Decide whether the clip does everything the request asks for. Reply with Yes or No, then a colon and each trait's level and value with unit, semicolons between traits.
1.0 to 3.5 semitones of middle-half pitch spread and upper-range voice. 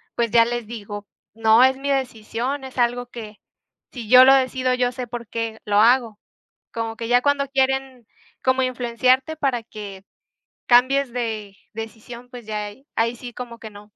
Yes: narrow, 2.4 semitones; high, 240 Hz